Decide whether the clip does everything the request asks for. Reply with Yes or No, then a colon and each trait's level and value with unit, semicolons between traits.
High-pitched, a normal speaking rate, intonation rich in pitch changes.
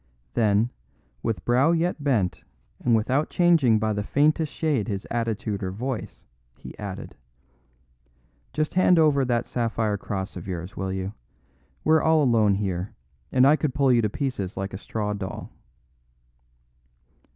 No: low, 115 Hz; average, 150 wpm; wide, 5.8 semitones